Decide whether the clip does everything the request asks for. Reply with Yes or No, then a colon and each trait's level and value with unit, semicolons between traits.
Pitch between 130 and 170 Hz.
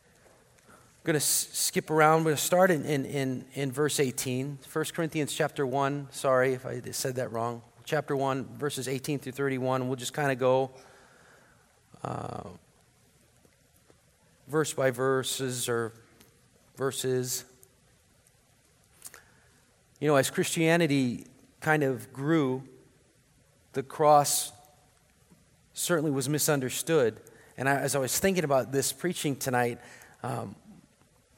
Yes: low, 135 Hz